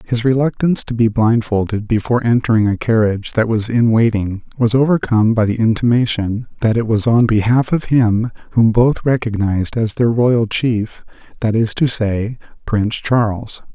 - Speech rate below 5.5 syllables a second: Yes, 5.0 syllables/s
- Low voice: Yes, low, 115 Hz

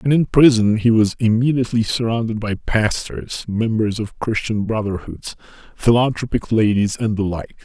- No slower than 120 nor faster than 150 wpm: Yes, average, 140 wpm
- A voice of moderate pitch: No, low, 110 Hz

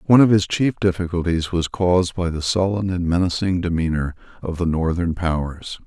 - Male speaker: Yes, male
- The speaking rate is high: No, average, 175 wpm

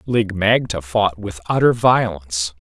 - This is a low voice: Yes, low, 100 Hz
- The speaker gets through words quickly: No, slow, 135 wpm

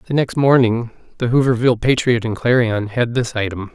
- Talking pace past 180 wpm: No, average, 175 wpm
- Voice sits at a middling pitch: No, low, 120 Hz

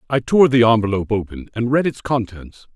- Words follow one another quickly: No, average, 195 wpm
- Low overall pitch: Yes, low, 115 Hz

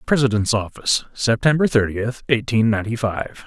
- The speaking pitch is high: No, low, 115 Hz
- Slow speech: Yes, slow, 120 wpm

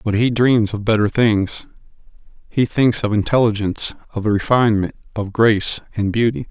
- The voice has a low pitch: Yes, low, 110 Hz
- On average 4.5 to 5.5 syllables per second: Yes, 5.1 syllables/s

